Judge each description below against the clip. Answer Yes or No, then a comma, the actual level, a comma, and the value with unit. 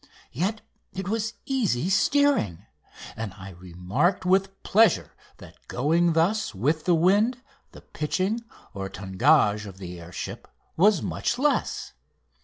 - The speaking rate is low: Yes, slow, 130 wpm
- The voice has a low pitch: No, medium, 165 Hz